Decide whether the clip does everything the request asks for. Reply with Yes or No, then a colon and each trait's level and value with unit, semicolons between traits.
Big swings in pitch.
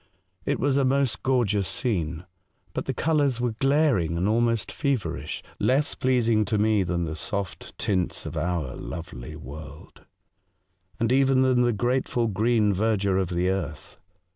Yes: wide, 6.3 semitones